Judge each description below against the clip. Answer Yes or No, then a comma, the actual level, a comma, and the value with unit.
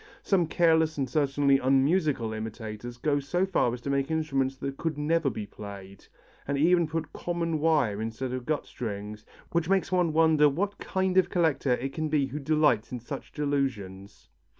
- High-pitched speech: No, medium, 140 Hz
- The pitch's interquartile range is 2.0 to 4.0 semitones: No, average, 4.8 semitones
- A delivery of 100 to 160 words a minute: No, average, 175 wpm